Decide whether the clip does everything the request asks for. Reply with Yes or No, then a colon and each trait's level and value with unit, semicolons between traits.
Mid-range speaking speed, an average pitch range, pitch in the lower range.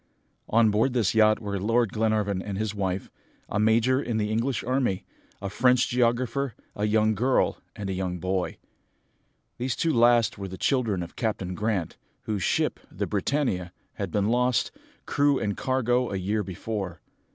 Yes: average, 165 wpm; average, 3.7 semitones; low, 110 Hz